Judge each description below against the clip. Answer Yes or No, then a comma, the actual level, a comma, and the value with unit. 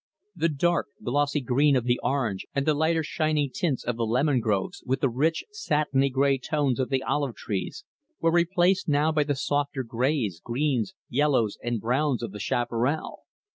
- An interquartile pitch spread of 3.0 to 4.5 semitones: Yes, average, 3.8 semitones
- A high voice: No, medium, 140 Hz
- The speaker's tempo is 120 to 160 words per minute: No, average, 175 wpm